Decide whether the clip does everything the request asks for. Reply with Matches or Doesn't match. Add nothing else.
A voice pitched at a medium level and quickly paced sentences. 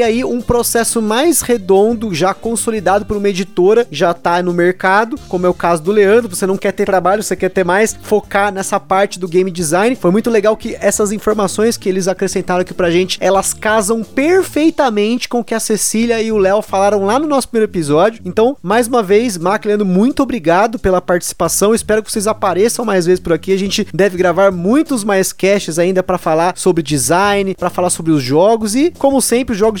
Doesn't match